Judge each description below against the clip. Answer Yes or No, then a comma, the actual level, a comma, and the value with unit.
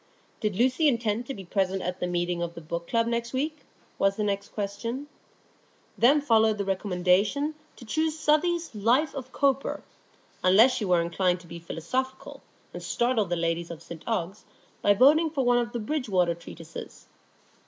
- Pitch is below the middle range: No, high, 215 Hz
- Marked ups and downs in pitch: Yes, wide, 6.3 semitones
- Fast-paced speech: No, average, 175 wpm